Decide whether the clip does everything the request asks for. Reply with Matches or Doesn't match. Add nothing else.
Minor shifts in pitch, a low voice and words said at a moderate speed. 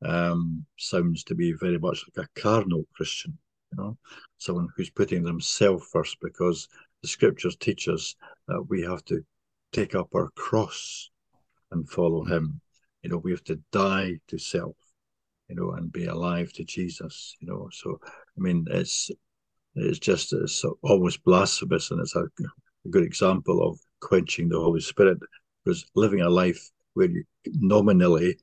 Matches